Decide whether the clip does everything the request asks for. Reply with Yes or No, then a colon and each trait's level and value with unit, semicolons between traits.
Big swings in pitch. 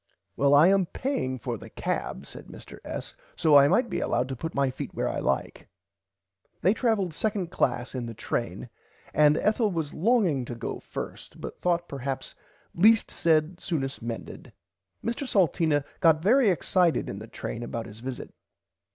Yes: wide, 6.5 semitones